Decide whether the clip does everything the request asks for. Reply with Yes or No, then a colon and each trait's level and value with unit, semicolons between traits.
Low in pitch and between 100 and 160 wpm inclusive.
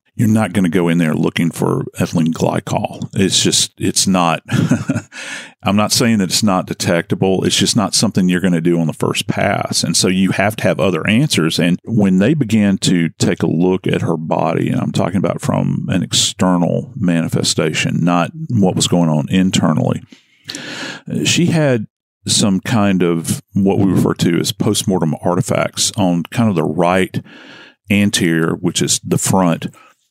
No: very low, 95 Hz; average, 175 wpm